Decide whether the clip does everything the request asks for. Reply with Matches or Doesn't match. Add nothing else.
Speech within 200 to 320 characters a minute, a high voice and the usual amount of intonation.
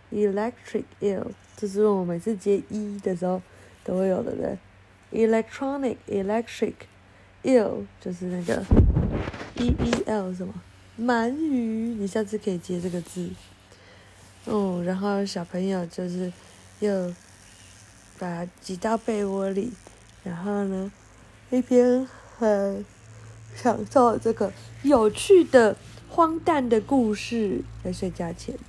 Matches